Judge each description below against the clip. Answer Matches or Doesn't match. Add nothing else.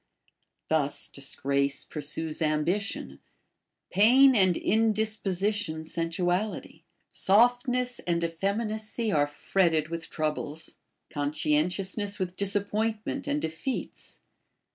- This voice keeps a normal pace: Doesn't match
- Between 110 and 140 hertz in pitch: Doesn't match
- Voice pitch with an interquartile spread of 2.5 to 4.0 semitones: Doesn't match